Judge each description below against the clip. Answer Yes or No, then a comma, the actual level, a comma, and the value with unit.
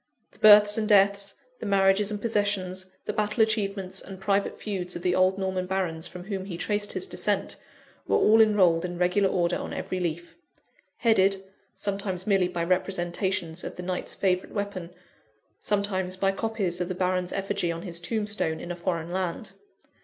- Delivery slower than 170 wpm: No, average, 175 wpm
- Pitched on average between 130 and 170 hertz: No, high, 190 Hz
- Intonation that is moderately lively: No, narrow, 2.2 semitones